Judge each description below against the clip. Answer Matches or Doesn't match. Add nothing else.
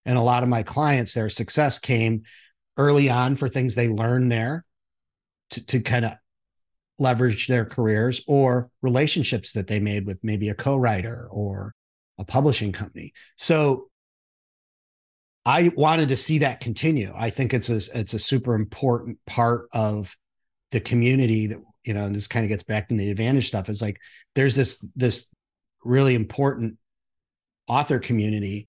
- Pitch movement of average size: Matches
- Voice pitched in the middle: Doesn't match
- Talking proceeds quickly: Doesn't match